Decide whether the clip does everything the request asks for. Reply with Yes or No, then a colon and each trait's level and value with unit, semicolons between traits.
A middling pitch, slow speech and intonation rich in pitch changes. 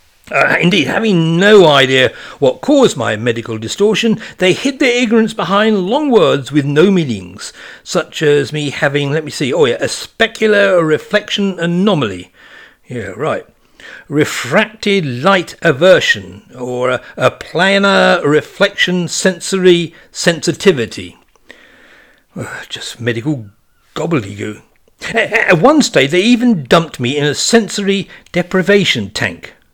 Yes: medium, 175 Hz; slow, 125 wpm; wide, 6.6 semitones